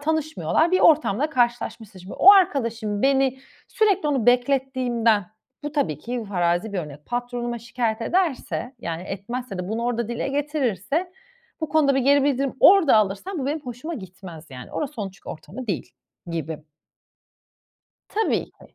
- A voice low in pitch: No, high, 245 Hz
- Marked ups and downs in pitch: Yes, wide, 5.8 semitones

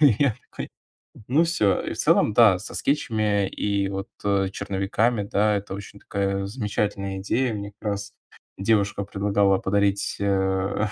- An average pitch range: No, narrow, 1.4 semitones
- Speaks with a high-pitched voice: No, low, 100 Hz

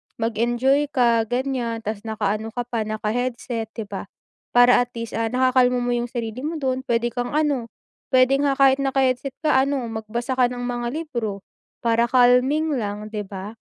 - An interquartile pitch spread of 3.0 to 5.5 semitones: No, narrow, 2.5 semitones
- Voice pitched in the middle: No, high, 245 Hz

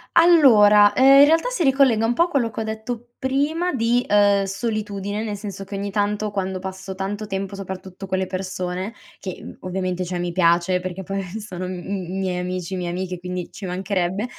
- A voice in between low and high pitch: No, high, 195 Hz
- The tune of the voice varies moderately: Yes, average, 3.2 semitones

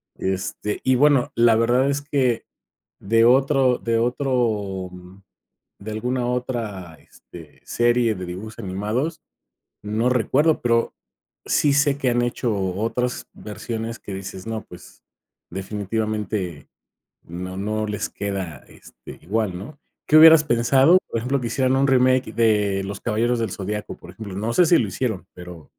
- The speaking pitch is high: No, low, 115 Hz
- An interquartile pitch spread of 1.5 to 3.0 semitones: No, average, 4.3 semitones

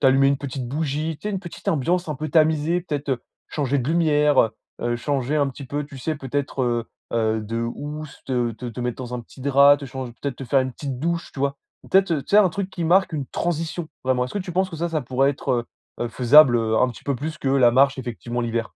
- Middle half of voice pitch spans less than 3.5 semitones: No, average, 3.8 semitones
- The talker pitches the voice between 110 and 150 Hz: Yes, medium, 140 Hz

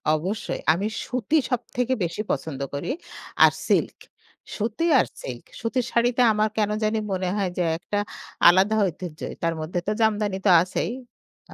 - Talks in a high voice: Yes, high, 210 Hz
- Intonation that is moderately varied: Yes, average, 3.9 semitones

